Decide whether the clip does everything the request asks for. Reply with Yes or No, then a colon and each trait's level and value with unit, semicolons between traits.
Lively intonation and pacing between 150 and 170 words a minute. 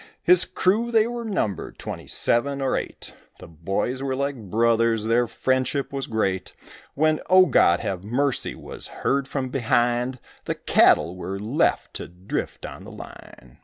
No: average, 4.5 semitones; average, 160 wpm